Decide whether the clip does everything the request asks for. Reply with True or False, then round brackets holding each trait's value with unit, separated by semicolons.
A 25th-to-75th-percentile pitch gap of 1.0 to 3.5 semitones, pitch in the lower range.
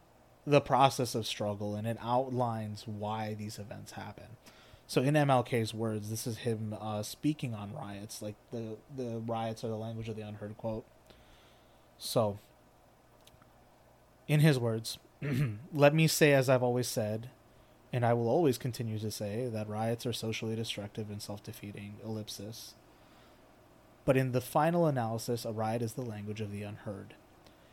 True (2.8 semitones; 115 Hz)